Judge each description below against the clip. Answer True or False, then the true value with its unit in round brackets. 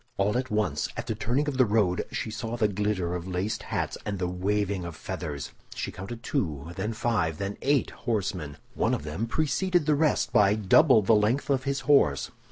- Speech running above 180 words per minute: True (200 wpm)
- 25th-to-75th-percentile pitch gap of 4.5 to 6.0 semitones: True (5.6 semitones)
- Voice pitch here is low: True (105 Hz)